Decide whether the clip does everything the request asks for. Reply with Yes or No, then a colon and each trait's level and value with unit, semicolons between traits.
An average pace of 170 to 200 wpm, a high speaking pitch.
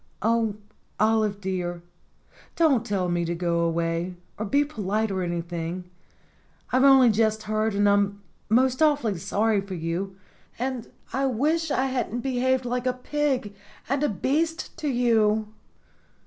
No: average, 150 wpm; high, 220 Hz